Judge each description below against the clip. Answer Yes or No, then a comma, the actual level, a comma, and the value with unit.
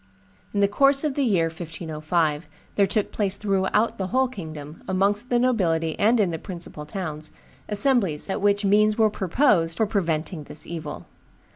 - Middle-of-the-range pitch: No, high, 195 Hz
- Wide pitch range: No, average, 4.5 semitones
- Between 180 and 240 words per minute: No, average, 165 wpm